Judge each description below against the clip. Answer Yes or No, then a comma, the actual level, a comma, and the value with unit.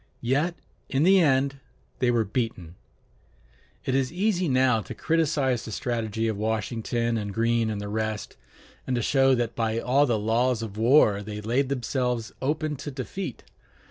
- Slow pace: No, average, 165 wpm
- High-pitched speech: No, low, 120 Hz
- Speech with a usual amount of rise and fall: Yes, average, 3.6 semitones